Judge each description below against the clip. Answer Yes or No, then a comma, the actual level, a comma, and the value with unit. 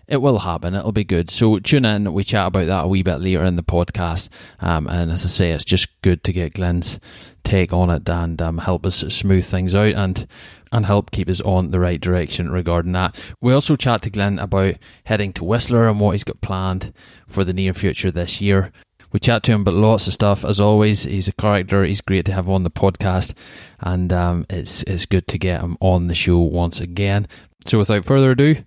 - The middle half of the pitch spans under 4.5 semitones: Yes, narrow, 2.6 semitones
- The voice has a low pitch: Yes, very low, 95 Hz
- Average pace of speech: No, fast, 230 wpm